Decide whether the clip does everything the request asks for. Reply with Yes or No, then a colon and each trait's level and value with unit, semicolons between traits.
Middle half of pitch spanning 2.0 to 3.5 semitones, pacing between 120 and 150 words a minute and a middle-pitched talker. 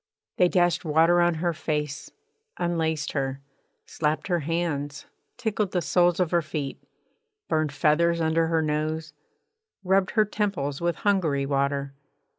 Yes: average, 2.7 semitones; slow, 135 wpm; medium, 160 Hz